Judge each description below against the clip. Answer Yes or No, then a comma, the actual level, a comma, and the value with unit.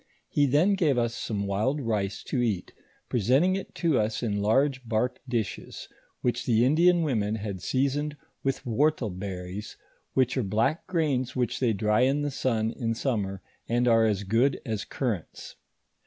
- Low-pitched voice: Yes, low, 120 Hz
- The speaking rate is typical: Yes, average, 165 wpm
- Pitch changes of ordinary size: Yes, average, 4.4 semitones